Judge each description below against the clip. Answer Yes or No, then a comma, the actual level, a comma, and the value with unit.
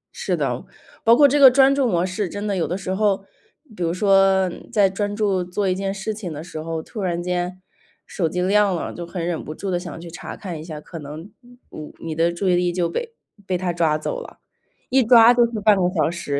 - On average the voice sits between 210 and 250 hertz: No, medium, 185 Hz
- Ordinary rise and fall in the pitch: Yes, average, 3.4 semitones